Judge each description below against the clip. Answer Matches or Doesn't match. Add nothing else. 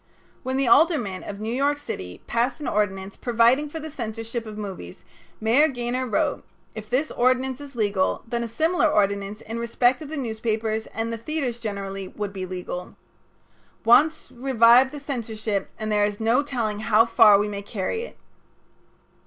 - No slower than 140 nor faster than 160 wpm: Doesn't match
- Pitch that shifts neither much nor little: Matches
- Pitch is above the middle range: Matches